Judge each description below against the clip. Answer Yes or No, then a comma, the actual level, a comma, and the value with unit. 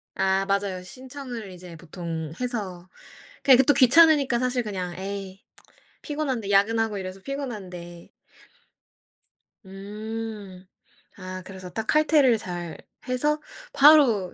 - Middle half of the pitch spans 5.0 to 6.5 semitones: Yes, average, 5.3 semitones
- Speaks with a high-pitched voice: Yes, high, 205 Hz